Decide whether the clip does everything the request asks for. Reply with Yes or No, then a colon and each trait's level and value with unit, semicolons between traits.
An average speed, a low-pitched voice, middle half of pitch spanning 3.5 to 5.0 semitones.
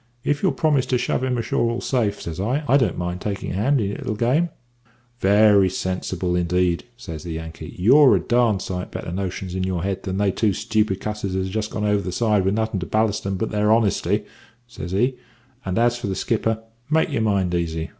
No: fast, 225 wpm; low, 105 Hz; average, 4.1 semitones